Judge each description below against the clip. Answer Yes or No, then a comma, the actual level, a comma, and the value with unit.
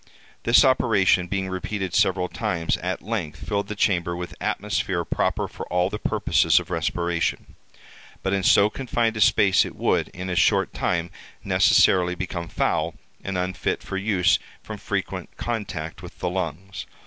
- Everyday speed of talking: Yes, average, 160 wpm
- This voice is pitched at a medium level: No, very low, 95 Hz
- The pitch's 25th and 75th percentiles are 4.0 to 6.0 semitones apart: No, narrow, 2.5 semitones